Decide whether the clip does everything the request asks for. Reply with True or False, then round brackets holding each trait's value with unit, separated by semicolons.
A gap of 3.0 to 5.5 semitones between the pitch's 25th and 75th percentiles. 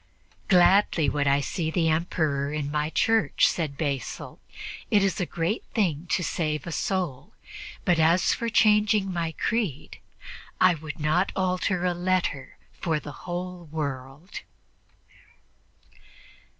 True (3.7 semitones)